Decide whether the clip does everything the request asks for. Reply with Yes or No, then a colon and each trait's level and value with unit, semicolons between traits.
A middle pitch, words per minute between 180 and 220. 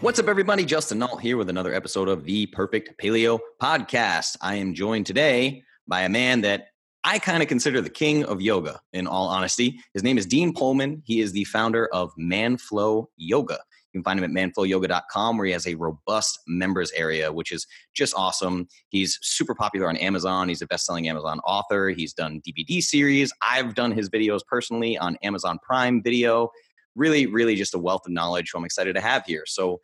No: low, 100 Hz; average, 200 wpm